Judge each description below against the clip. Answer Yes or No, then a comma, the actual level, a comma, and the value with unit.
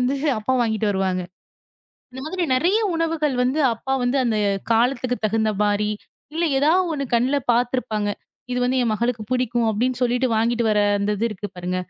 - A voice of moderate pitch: No, high, 240 Hz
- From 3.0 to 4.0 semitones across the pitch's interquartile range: Yes, average, 3.4 semitones